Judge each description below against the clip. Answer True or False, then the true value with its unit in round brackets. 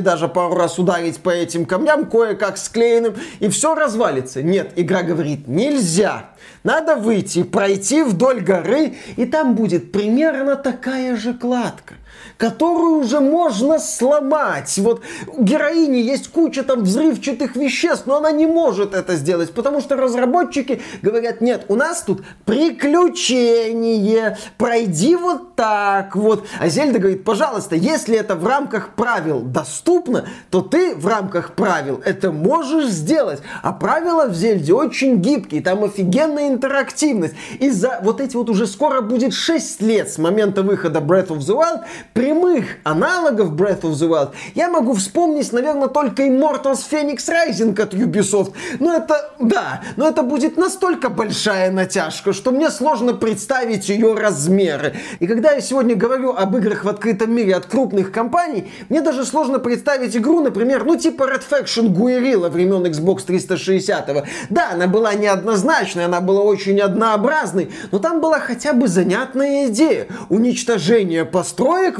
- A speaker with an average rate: True (150 wpm)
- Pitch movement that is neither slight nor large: False (6.5 semitones)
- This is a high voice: True (230 Hz)